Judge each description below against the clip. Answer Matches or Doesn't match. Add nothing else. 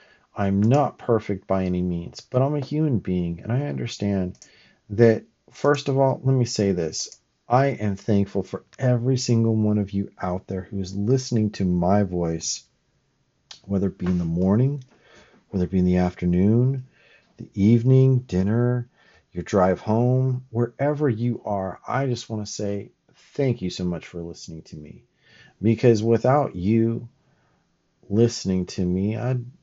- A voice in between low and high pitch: Doesn't match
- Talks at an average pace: Matches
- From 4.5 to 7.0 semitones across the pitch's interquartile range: Matches